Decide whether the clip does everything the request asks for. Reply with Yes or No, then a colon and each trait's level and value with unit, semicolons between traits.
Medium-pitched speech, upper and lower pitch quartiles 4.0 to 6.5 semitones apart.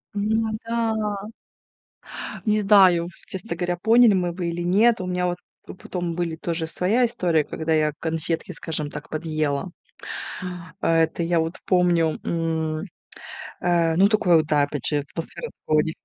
No: medium, 175 Hz; average, 2.9 semitones